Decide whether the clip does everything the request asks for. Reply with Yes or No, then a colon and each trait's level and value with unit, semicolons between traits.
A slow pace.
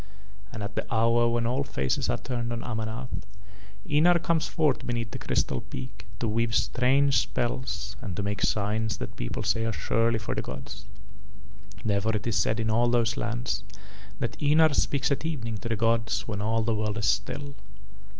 No: average, 185 wpm